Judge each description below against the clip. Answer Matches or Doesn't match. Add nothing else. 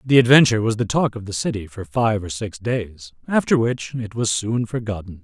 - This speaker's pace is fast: Matches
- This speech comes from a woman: Doesn't match